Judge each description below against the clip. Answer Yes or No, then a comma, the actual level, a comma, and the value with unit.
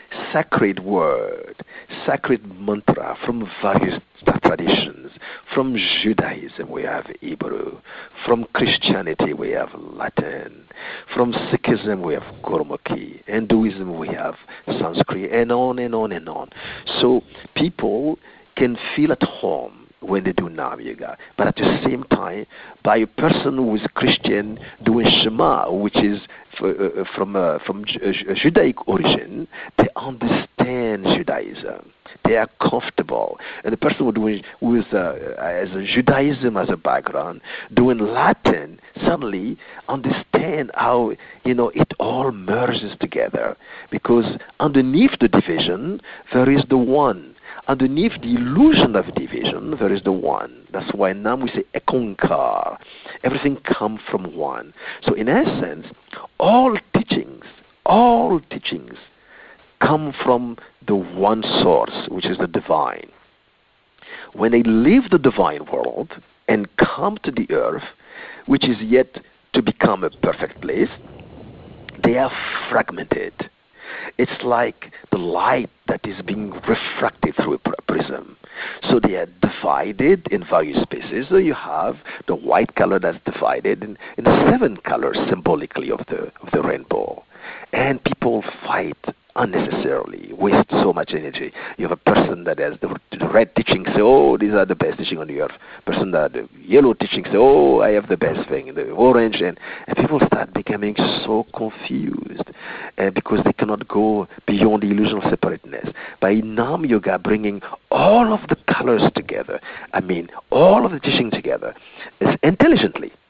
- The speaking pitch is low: Yes, low, 125 Hz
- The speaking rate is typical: Yes, average, 145 wpm